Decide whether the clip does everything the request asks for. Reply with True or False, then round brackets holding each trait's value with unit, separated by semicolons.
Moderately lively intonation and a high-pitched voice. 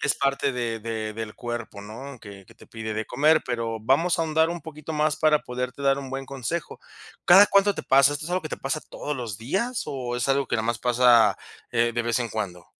False (4.9 semitones; 125 Hz)